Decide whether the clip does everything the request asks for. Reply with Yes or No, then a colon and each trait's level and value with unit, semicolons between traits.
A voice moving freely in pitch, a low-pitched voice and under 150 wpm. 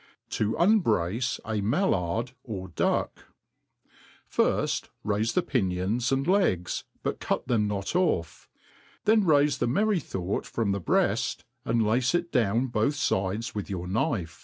Yes: wide, 6.4 semitones; low, 115 Hz; average, 140 wpm